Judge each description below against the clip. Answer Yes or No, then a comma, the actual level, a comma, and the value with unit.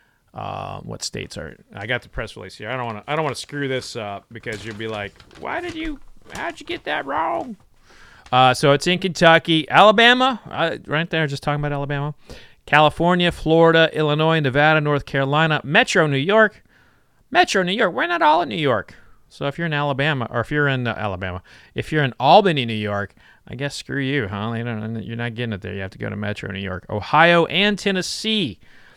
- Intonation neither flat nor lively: No, wide, 6.3 semitones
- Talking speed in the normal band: No, fast, 215 wpm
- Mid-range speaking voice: Yes, medium, 145 Hz